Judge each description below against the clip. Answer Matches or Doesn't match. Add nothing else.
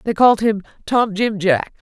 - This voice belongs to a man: Doesn't match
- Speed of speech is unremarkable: Matches